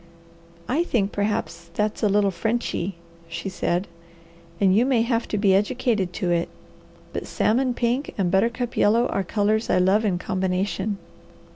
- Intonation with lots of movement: No, average, 3.6 semitones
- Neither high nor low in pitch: No, high, 205 Hz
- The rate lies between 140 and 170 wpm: Yes, average, 155 wpm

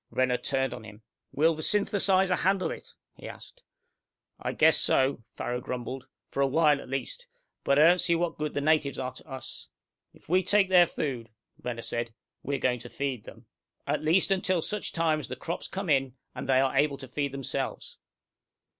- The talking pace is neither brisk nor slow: Yes, average, 195 wpm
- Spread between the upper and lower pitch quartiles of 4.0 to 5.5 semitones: Yes, average, 5.0 semitones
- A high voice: No, medium, 145 Hz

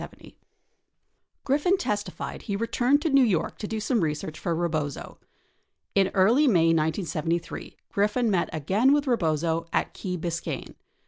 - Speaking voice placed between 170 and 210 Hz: Yes, high, 190 Hz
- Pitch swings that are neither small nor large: No, wide, 6.5 semitones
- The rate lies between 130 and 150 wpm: Yes, average, 145 wpm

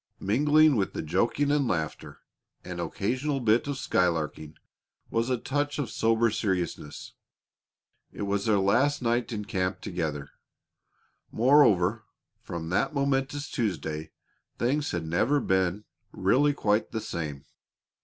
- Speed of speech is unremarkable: No, slow, 125 wpm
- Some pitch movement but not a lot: No, wide, 7.1 semitones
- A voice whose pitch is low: Yes, low, 110 Hz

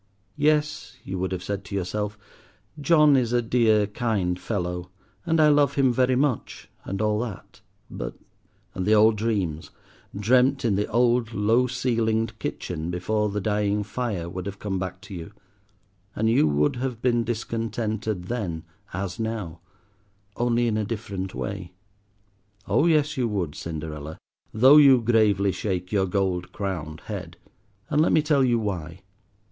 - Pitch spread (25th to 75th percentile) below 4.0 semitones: No, average, 4.4 semitones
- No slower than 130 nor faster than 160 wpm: Yes, average, 155 wpm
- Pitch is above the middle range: No, low, 105 Hz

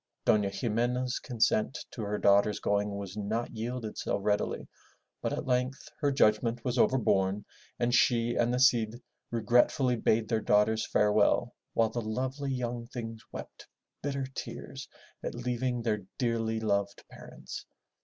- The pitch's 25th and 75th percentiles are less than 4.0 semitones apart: Yes, average, 2.7 semitones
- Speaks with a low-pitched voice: Yes, low, 115 Hz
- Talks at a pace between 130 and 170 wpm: Yes, average, 145 wpm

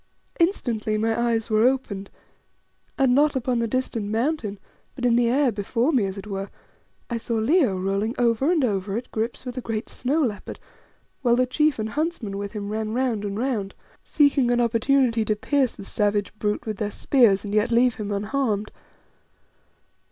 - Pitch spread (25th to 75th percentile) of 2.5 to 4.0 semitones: Yes, average, 3.5 semitones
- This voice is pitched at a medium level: No, high, 230 Hz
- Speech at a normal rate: Yes, average, 180 wpm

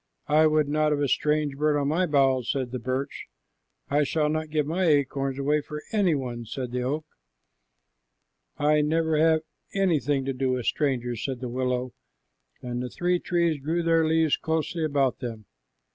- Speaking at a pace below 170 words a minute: No, average, 175 wpm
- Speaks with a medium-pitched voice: Yes, medium, 145 Hz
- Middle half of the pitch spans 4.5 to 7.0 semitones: No, average, 3.3 semitones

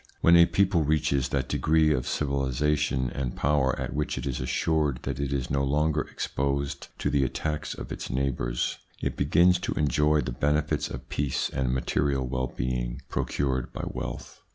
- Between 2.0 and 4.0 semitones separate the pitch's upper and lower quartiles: Yes, narrow, 2.5 semitones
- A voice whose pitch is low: Yes, very low, 70 Hz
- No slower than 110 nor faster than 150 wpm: No, average, 175 wpm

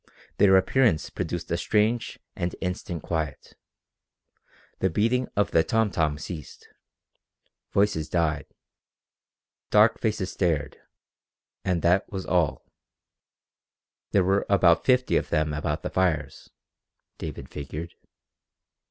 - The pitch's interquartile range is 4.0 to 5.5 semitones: Yes, average, 4.5 semitones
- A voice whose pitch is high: No, very low, 90 Hz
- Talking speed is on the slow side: Yes, slow, 110 wpm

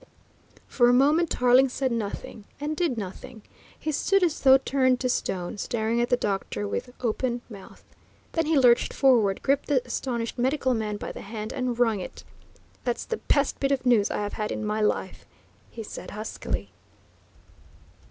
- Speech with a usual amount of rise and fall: Yes, average, 3.9 semitones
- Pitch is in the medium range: No, high, 245 Hz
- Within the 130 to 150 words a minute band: No, average, 175 wpm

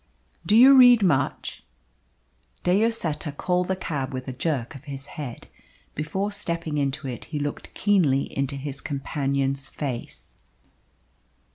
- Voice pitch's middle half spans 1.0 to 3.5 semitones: No, average, 4.7 semitones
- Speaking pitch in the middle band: Yes, medium, 145 Hz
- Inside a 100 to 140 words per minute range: Yes, slow, 135 wpm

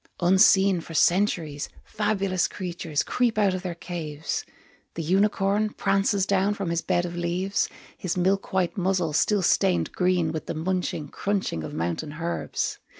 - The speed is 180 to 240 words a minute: No, average, 150 wpm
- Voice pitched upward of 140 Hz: Yes, medium, 185 Hz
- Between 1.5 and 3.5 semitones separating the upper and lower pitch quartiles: Yes, average, 2.7 semitones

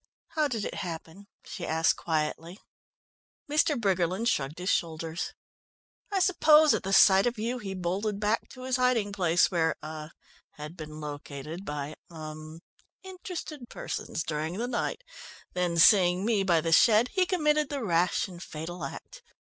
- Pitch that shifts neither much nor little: No, wide, 6.9 semitones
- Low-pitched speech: No, medium, 185 Hz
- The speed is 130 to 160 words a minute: Yes, average, 155 wpm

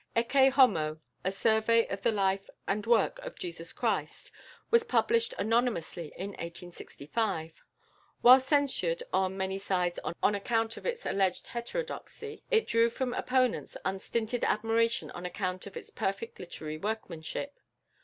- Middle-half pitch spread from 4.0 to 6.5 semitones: Yes, average, 5.3 semitones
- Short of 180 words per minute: Yes, slow, 135 wpm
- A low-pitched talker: No, high, 225 Hz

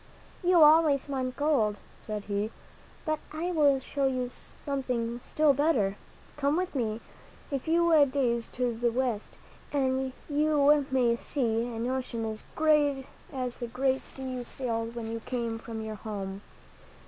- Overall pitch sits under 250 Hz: No, very high, 255 Hz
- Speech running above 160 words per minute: No, average, 150 wpm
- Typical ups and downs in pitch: Yes, average, 4.0 semitones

